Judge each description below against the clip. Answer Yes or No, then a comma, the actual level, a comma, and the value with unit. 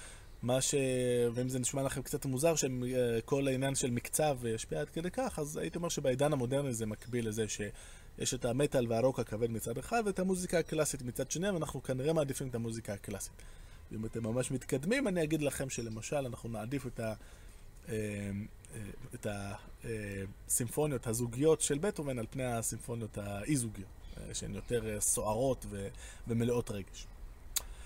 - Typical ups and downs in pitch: Yes, average, 4.7 semitones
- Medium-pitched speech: No, low, 120 Hz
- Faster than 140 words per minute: Yes, fast, 150 wpm